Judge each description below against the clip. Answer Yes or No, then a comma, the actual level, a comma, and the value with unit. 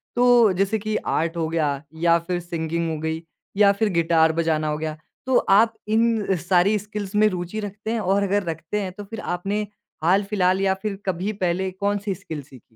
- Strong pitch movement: No, average, 3.8 semitones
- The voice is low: No, high, 190 Hz